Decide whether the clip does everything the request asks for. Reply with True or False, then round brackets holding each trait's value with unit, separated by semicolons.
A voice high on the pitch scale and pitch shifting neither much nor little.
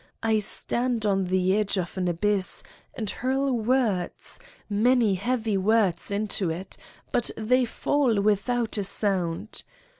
True (210 Hz; 3.8 semitones)